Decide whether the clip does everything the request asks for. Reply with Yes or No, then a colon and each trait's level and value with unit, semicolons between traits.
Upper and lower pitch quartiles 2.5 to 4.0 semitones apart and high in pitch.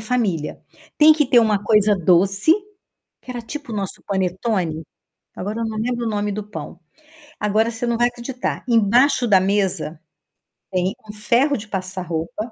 Yes: average, 3.7 semitones; high, 210 Hz